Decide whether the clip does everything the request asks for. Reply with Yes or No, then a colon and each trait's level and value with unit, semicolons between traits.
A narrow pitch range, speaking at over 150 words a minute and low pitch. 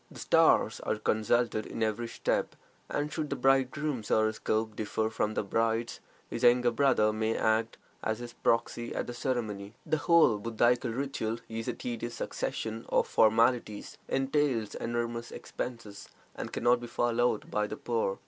Yes: narrow, 2.0 semitones; average, 160 wpm; low, 115 Hz